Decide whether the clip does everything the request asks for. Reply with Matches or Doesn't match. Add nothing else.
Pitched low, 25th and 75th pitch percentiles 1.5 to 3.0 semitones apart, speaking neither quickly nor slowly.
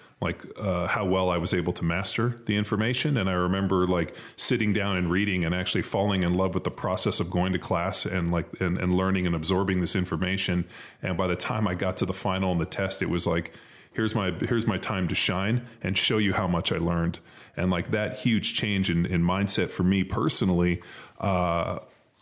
Doesn't match